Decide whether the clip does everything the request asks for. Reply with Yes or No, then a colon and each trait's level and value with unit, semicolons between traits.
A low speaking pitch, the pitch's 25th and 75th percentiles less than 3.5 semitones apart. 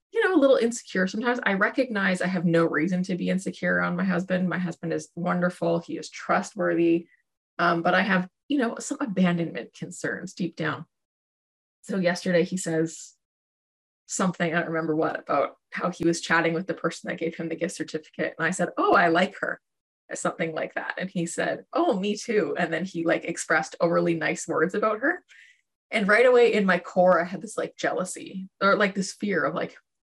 No: medium, 175 Hz; average, 2.8 semitones